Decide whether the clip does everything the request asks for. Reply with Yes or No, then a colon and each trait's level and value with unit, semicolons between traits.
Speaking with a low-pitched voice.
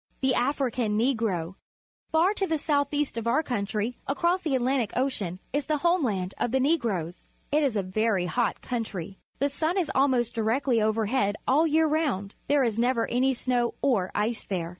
No: high, 245 Hz